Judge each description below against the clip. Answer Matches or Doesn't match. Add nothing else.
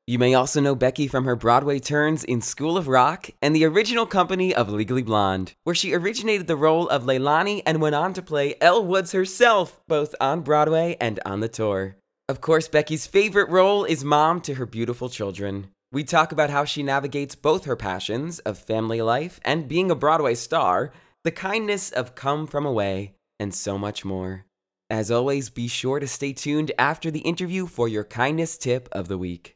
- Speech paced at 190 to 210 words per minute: Matches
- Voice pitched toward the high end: Doesn't match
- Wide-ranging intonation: Matches